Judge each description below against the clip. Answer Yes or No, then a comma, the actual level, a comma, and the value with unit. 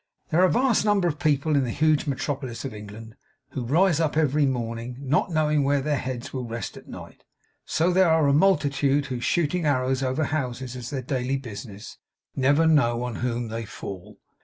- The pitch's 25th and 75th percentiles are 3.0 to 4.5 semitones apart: Yes, average, 4.1 semitones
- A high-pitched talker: No, low, 135 Hz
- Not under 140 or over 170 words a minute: No, average, 200 wpm